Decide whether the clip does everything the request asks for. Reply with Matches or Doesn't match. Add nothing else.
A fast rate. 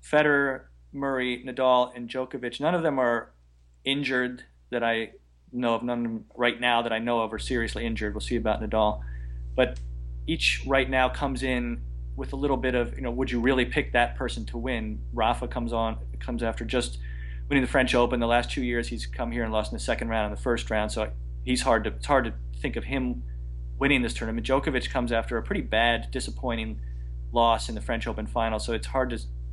Matches